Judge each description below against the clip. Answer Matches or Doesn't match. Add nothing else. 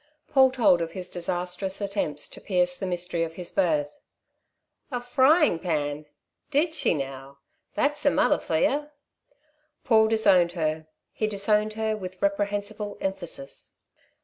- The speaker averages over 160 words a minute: Doesn't match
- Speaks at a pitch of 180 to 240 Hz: Matches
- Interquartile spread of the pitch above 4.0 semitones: Matches